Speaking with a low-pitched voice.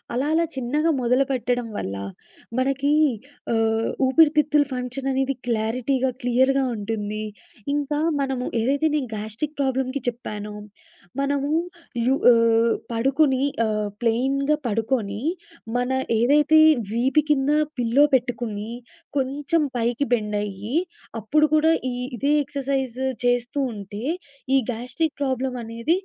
No: very high, 255 Hz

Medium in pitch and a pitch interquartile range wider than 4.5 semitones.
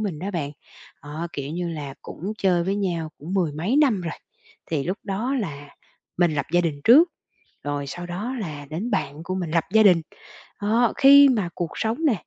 Yes: medium, 175 Hz; average, 5.1 semitones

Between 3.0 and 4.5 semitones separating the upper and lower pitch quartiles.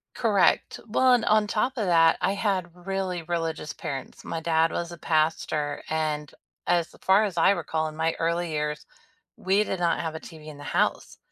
Yes: average, 3.5 semitones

